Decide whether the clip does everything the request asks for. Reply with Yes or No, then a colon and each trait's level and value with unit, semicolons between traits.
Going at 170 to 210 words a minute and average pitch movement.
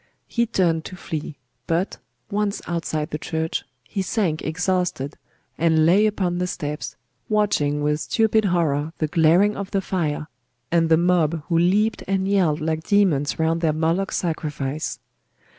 No: average, 150 wpm; average, 3.5 semitones